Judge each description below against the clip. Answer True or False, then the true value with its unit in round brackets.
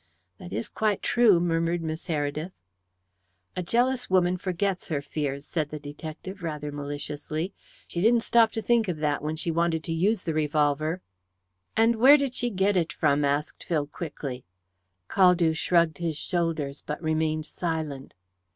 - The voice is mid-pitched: True (165 Hz)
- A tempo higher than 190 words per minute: False (160 wpm)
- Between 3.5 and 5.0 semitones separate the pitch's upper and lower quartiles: True (3.8 semitones)